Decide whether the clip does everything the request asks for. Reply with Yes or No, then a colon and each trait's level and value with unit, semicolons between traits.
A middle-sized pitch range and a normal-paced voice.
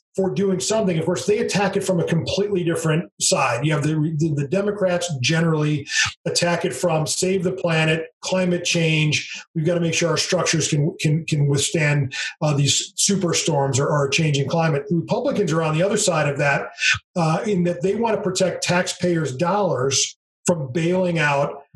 Yes: average, 3.3 semitones; average, 190 wpm